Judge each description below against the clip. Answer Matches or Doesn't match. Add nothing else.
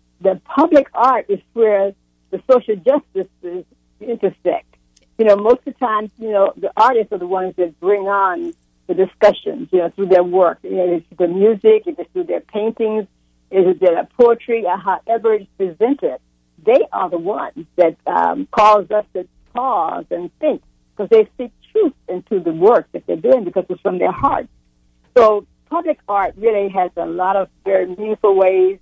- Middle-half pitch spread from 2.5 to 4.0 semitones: Doesn't match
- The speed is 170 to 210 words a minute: Matches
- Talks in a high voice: Matches